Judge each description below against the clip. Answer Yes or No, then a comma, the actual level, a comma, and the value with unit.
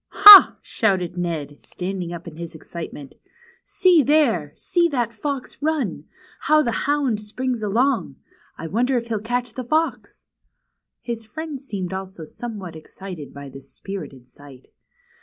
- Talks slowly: No, average, 145 wpm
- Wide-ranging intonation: Yes, wide, 7.5 semitones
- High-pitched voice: Yes, high, 210 Hz